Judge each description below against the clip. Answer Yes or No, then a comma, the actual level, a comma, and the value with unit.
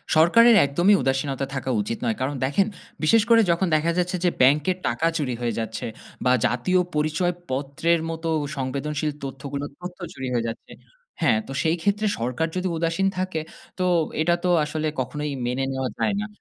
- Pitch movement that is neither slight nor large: Yes, average, 4.9 semitones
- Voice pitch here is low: No, medium, 150 Hz